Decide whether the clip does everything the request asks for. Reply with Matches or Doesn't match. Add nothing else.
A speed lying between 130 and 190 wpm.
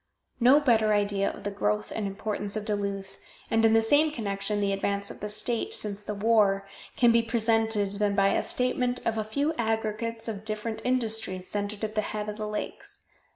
Doesn't match